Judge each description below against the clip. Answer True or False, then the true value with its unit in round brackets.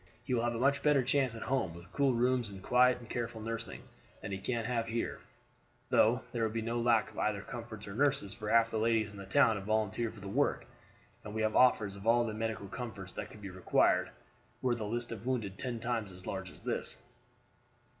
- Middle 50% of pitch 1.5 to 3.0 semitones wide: True (2.7 semitones)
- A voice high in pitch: False (115 Hz)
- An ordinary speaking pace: False (235 wpm)